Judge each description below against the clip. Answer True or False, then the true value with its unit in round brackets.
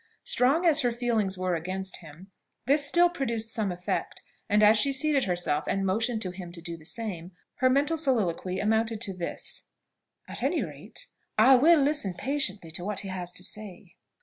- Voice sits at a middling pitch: False (210 Hz)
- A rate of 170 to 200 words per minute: True (185 wpm)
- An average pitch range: False (6.2 semitones)